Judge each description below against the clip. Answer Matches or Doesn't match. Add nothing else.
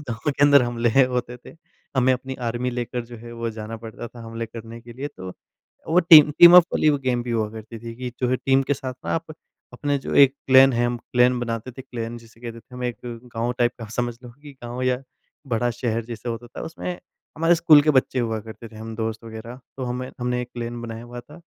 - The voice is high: Doesn't match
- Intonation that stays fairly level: Matches